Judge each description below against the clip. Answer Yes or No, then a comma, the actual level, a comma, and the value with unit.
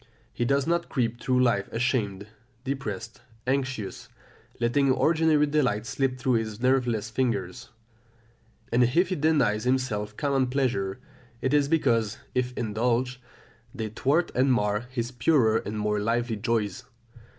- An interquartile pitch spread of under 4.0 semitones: Yes, average, 3.5 semitones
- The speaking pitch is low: Yes, low, 125 Hz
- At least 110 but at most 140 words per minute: Yes, slow, 135 wpm